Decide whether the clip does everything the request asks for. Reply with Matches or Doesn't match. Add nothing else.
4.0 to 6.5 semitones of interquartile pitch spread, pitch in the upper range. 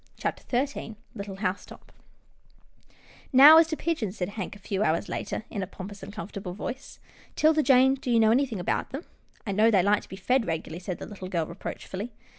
Matches